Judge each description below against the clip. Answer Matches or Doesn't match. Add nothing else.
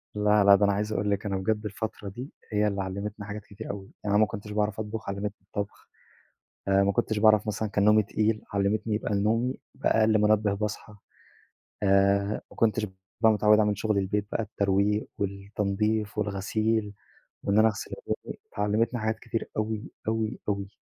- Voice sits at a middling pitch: Doesn't match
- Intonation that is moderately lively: Doesn't match